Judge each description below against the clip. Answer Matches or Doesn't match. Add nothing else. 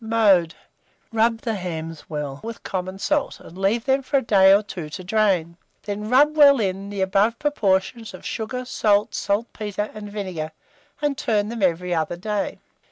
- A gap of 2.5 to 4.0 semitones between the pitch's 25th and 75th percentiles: Matches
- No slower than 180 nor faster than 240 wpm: Doesn't match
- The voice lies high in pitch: Matches